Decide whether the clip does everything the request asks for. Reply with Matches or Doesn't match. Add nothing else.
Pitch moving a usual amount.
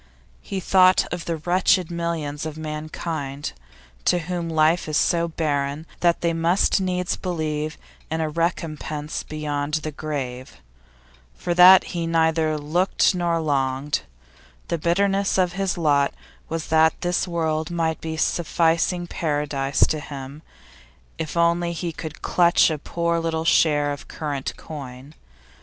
Doesn't match